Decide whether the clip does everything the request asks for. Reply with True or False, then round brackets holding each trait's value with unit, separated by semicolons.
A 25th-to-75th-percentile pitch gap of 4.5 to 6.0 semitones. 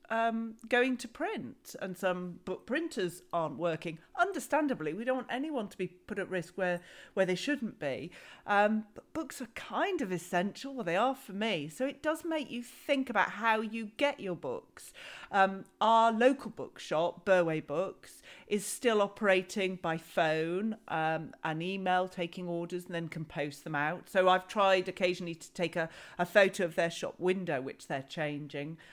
True (5.3 semitones)